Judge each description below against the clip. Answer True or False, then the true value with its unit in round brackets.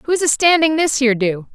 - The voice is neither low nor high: False (280 Hz)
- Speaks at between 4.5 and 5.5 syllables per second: True (5.4 syllables/s)